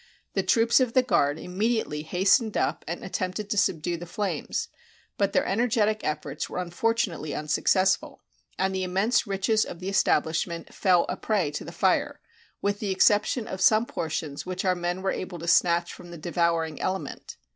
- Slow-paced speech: No, average, 180 wpm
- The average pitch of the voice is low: No, medium, 185 Hz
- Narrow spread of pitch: No, average, 3.6 semitones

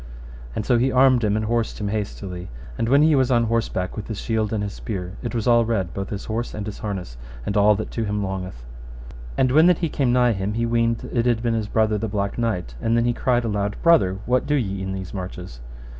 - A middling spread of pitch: Yes, average, 3.2 semitones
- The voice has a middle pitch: No, low, 110 Hz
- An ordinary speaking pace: No, fast, 250 wpm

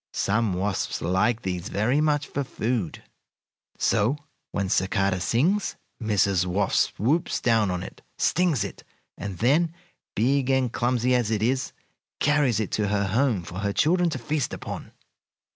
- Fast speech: No, average, 150 wpm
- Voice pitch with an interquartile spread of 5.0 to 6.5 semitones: Yes, wide, 5.6 semitones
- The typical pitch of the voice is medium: No, low, 115 Hz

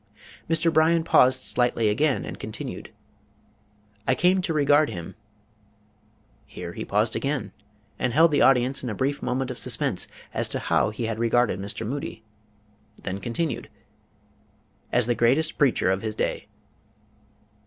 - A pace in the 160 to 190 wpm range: No, average, 145 wpm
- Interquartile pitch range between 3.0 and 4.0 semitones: No, average, 4.8 semitones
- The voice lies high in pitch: No, low, 125 Hz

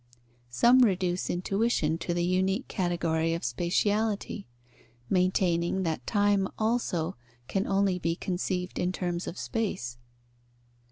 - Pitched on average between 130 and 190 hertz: Yes, medium, 185 Hz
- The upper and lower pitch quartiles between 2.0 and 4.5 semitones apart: Yes, average, 2.7 semitones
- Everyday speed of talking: No, slow, 115 wpm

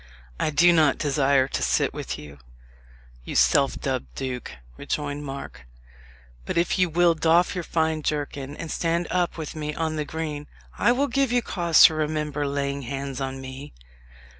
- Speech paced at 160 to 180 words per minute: Yes, average, 170 wpm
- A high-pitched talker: No, medium, 150 Hz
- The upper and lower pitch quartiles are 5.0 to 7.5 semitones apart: No, average, 3.0 semitones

